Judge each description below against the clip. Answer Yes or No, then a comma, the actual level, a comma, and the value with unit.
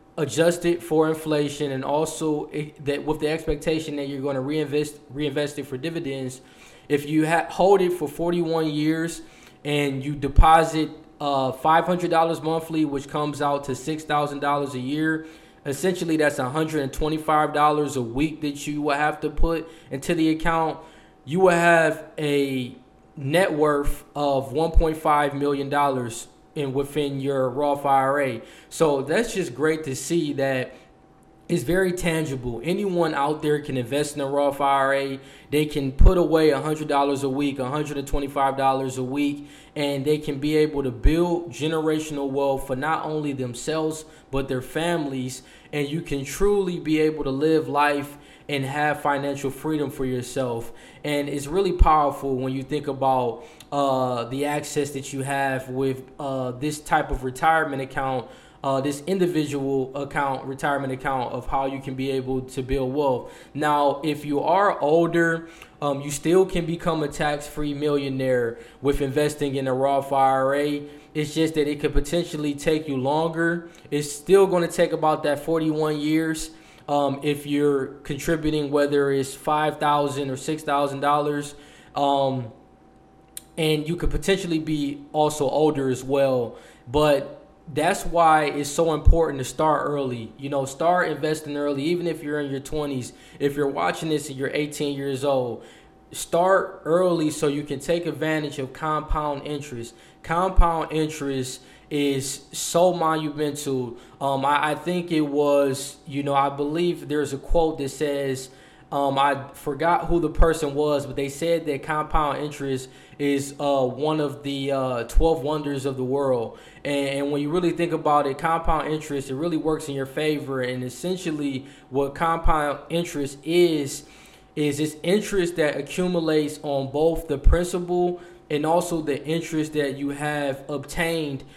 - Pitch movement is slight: Yes, narrow, 2.2 semitones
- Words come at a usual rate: Yes, average, 160 wpm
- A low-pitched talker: No, medium, 145 Hz